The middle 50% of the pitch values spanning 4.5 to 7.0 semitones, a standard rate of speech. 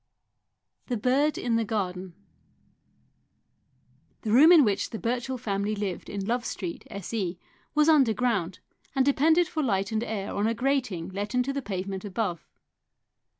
Yes: average, 4.8 semitones; average, 150 wpm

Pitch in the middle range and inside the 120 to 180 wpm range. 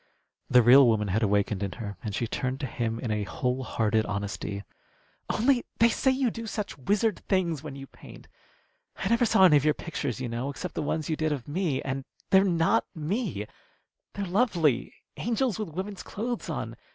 No: medium, 150 Hz; average, 195 wpm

